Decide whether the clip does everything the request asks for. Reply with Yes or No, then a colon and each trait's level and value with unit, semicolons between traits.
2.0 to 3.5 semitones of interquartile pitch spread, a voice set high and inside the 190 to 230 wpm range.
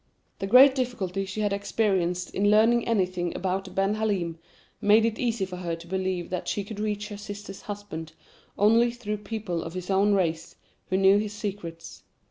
No: average, 2.7 semitones; high, 200 Hz; average, 180 wpm